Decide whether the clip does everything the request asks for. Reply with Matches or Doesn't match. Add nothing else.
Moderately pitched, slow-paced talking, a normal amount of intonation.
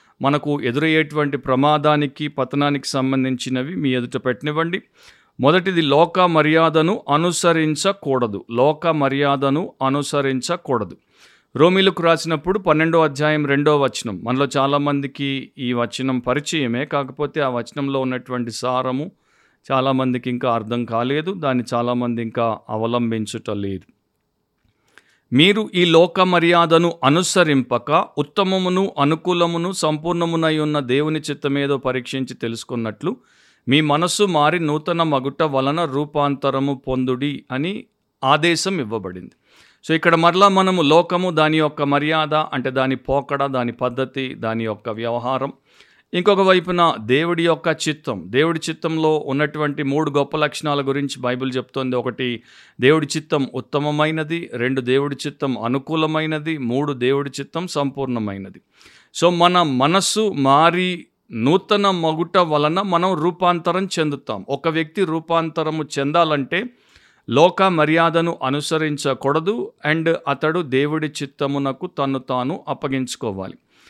Doesn't match